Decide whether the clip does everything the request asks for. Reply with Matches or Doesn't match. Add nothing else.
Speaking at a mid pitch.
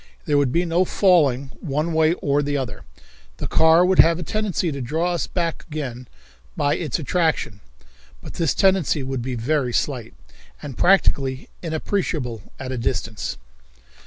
Matches